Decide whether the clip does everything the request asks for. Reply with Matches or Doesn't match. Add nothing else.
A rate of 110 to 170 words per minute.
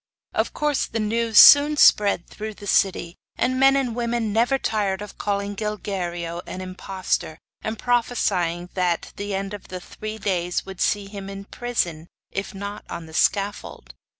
Matches